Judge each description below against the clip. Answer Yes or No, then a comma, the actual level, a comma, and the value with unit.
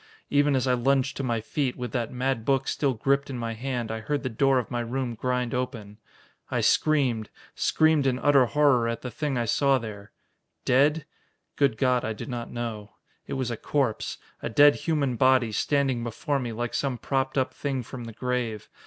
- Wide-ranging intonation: No, average, 2.8 semitones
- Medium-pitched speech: No, low, 125 Hz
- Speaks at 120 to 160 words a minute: No, average, 200 wpm